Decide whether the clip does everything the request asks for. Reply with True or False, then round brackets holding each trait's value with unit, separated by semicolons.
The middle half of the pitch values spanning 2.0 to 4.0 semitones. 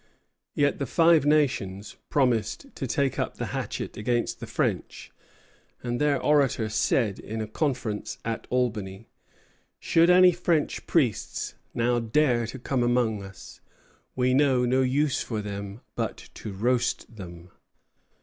False (4.5 semitones)